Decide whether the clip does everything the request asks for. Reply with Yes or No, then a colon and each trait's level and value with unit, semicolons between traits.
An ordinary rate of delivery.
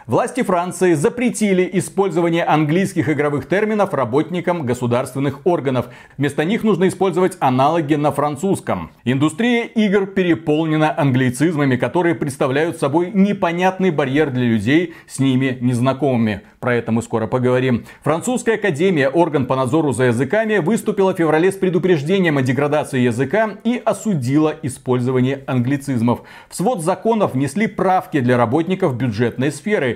Yes: average, 130 wpm